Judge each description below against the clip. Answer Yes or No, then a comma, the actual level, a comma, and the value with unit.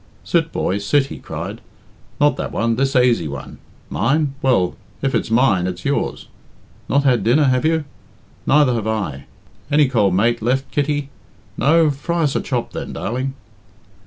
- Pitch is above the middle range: No, low, 130 Hz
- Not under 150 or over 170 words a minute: Yes, average, 160 wpm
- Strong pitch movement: No, average, 4.4 semitones